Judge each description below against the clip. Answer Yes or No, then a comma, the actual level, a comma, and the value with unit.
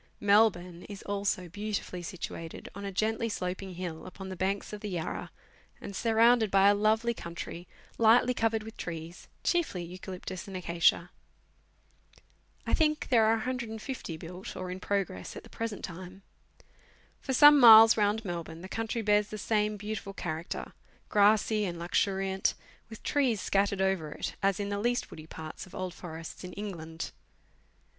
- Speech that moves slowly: No, average, 160 wpm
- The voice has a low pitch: No, high, 200 Hz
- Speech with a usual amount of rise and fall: Yes, average, 3.4 semitones